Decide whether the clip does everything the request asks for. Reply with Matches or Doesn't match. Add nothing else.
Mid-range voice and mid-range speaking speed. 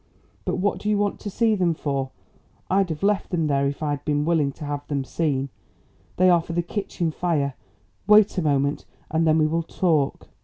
Doesn't match